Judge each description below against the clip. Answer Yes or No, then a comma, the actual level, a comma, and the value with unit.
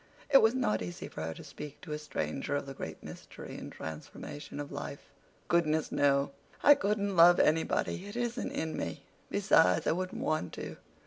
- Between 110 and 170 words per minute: No, average, 185 wpm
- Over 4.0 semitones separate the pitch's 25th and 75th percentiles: Yes, wide, 5.4 semitones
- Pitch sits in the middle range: Yes, medium, 150 Hz